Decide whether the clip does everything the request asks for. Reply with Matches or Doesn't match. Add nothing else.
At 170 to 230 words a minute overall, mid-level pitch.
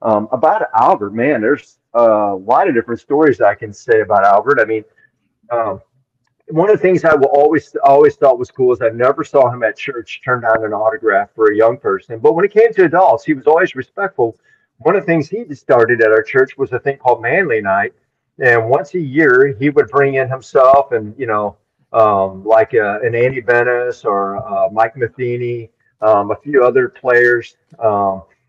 Doesn't match